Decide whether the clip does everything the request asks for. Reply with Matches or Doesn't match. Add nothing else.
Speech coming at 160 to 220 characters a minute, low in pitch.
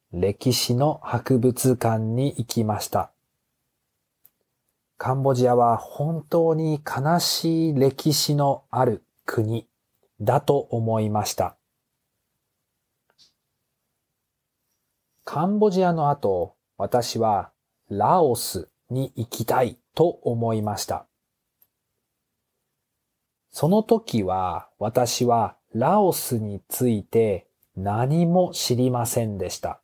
Matches